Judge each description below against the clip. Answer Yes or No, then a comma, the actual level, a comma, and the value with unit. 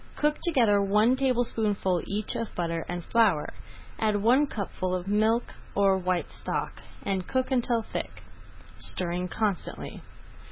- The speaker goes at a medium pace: No, slow, 130 wpm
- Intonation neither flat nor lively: Yes, average, 4.2 semitones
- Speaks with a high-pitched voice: Yes, high, 210 Hz